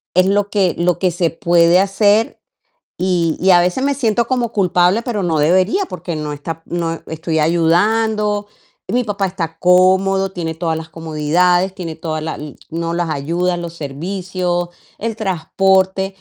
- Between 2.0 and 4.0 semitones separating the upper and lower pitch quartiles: Yes, average, 2.9 semitones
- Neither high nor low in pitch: Yes, medium, 180 Hz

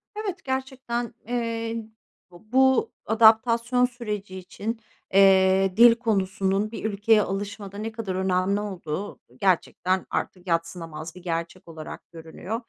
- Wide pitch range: No, average, 3.7 semitones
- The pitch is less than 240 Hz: Yes, high, 205 Hz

